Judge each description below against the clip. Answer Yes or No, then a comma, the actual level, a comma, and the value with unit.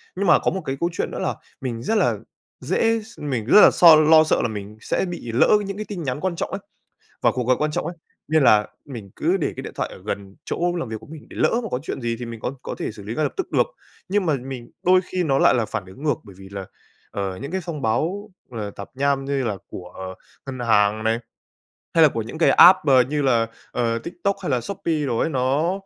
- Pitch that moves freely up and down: Yes, wide, 7.0 semitones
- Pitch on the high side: No, low, 135 Hz